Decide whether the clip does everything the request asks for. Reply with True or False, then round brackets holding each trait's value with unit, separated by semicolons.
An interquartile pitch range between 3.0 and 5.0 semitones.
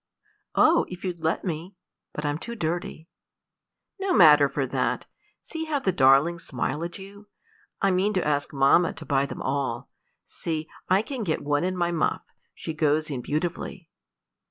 True (4.3 semitones)